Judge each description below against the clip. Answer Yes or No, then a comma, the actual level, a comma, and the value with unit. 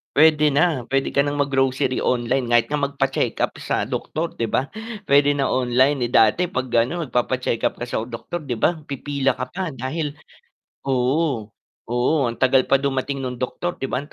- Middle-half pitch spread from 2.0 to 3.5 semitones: Yes, narrow, 2.5 semitones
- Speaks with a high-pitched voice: No, low, 135 Hz